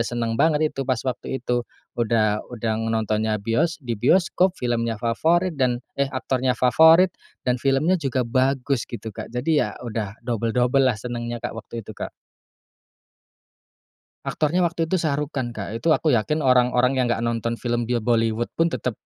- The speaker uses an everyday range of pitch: Yes, average, 3.4 semitones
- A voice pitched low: Yes, low, 125 Hz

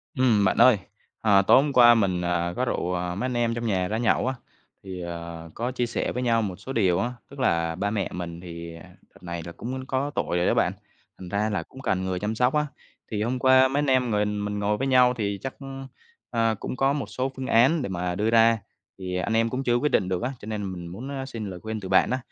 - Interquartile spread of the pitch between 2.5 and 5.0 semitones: No, wide, 5.5 semitones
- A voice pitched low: Yes, low, 110 Hz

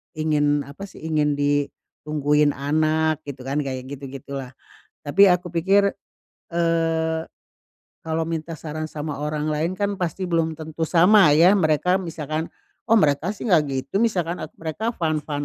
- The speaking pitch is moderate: Yes, medium, 155 Hz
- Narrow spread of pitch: Yes, narrow, 2.3 semitones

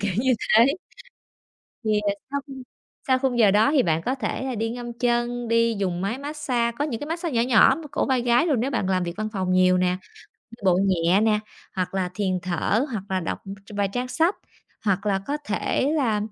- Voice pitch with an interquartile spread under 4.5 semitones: No, average, 4.9 semitones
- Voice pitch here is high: Yes, high, 225 Hz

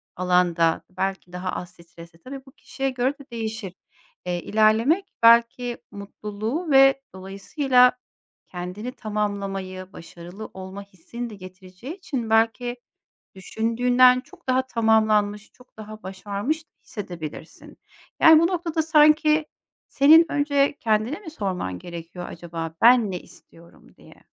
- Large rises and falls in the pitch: Yes, wide, 5.7 semitones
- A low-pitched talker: No, high, 215 Hz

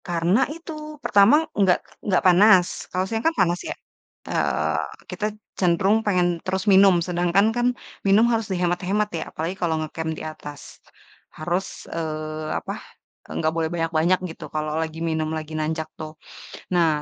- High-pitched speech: No, medium, 175 Hz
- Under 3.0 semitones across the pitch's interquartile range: No, average, 3.4 semitones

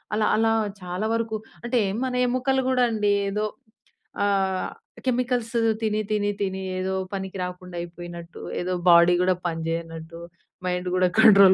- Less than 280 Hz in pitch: Yes, high, 190 Hz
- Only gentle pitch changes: No, average, 3.6 semitones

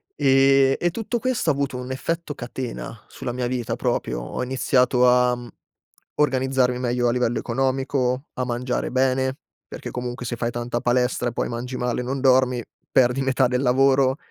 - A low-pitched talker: Yes, low, 125 Hz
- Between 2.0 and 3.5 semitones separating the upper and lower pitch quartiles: No, narrow, 1.5 semitones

